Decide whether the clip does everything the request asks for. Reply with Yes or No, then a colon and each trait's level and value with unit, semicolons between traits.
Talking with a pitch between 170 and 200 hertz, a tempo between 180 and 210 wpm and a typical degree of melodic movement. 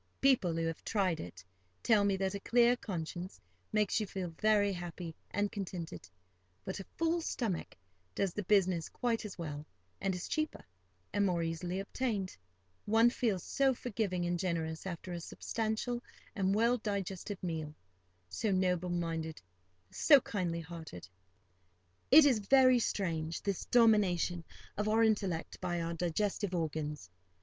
No: high, 190 Hz; average, 140 wpm; average, 4.4 semitones